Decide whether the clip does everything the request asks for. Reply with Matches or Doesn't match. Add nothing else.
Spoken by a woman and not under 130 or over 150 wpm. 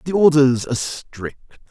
Doesn't match